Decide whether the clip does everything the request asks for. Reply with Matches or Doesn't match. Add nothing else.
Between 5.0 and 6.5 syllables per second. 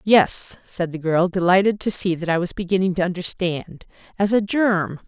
Doesn't match